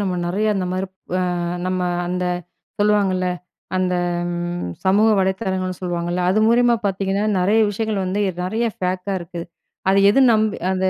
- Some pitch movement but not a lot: No, narrow, 2.2 semitones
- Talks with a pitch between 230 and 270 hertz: No, high, 190 Hz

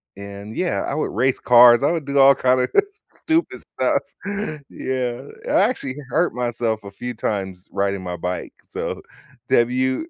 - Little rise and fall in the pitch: No, average, 5.0 semitones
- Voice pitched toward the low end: Yes, low, 125 Hz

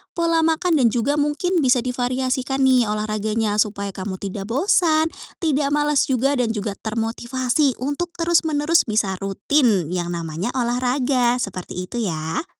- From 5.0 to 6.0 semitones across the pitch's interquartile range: Yes, wide, 5.5 semitones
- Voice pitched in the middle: No, high, 245 Hz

